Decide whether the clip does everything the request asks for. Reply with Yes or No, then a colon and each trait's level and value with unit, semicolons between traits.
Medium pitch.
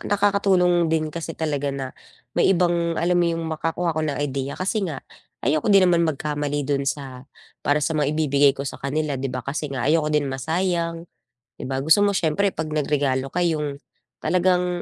Yes: medium, 155 Hz